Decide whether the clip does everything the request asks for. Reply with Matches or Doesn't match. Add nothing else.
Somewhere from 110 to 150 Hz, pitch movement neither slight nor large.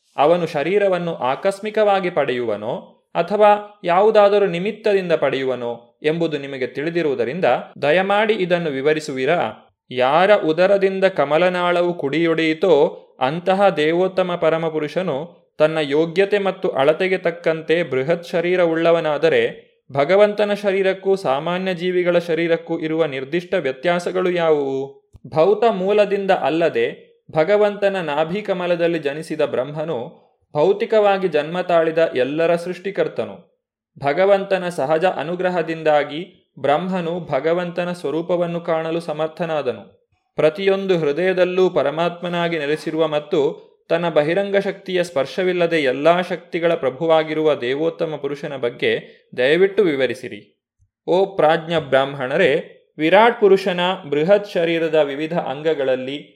Doesn't match